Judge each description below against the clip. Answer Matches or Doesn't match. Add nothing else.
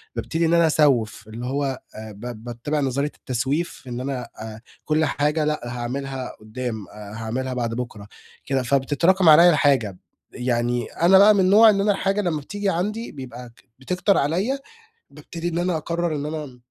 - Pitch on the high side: Doesn't match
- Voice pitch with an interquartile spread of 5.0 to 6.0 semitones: Matches